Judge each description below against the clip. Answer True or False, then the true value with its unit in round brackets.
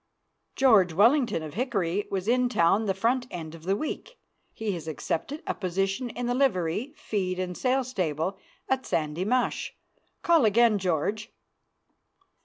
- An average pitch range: False (5.8 semitones)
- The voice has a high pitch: True (205 Hz)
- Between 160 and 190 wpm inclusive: False (150 wpm)